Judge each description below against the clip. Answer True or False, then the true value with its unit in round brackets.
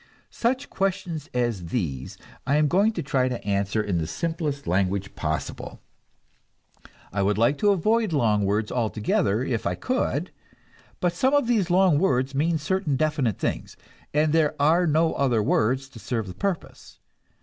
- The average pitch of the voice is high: False (140 Hz)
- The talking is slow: False (155 wpm)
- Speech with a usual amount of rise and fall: False (8.3 semitones)